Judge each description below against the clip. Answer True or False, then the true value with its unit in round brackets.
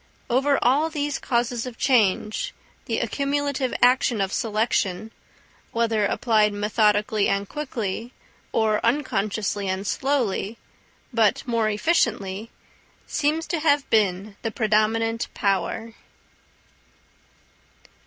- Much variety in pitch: False (3.8 semitones)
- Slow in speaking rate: True (100 wpm)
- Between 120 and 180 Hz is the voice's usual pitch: False (225 Hz)